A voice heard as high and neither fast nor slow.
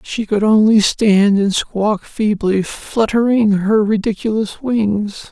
No: high, 215 Hz; slow, 125 wpm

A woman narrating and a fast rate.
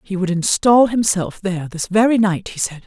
Yes: female; fast, 210 wpm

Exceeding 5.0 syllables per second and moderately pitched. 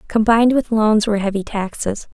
No: 5.6 syllables/s; high, 215 Hz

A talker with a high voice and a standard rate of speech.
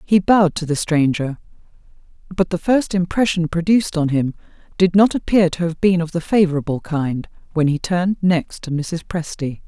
No: medium, 170 Hz; average, 180 wpm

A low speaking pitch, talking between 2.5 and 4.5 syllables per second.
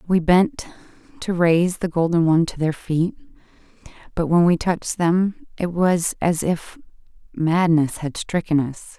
No: medium, 170 Hz; 4.4 syllables/s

